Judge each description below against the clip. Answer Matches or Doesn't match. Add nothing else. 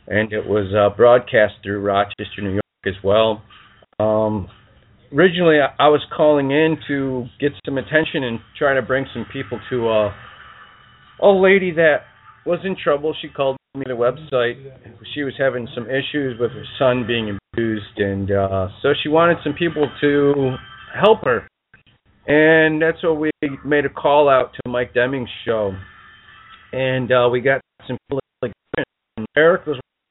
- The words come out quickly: Doesn't match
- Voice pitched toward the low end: Matches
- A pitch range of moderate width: Matches